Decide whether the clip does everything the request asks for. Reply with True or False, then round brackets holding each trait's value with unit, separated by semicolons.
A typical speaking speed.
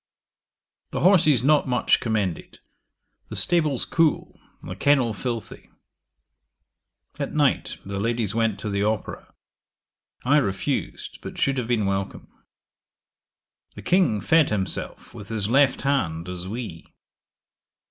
False (120 wpm)